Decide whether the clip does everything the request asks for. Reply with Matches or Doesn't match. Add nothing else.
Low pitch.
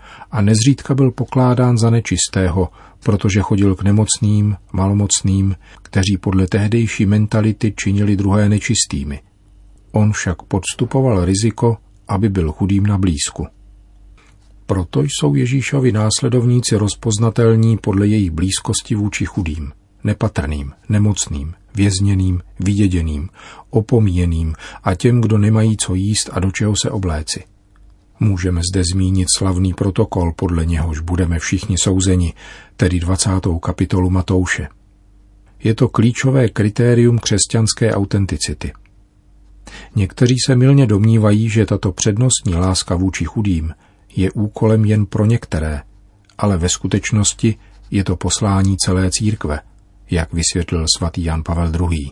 Matches